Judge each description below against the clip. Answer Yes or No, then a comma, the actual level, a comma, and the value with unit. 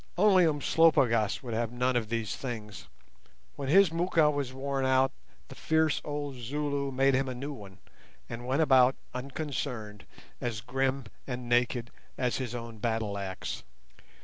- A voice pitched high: No, low, 130 Hz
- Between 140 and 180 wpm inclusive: Yes, average, 150 wpm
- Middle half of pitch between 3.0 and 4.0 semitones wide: Yes, average, 3.3 semitones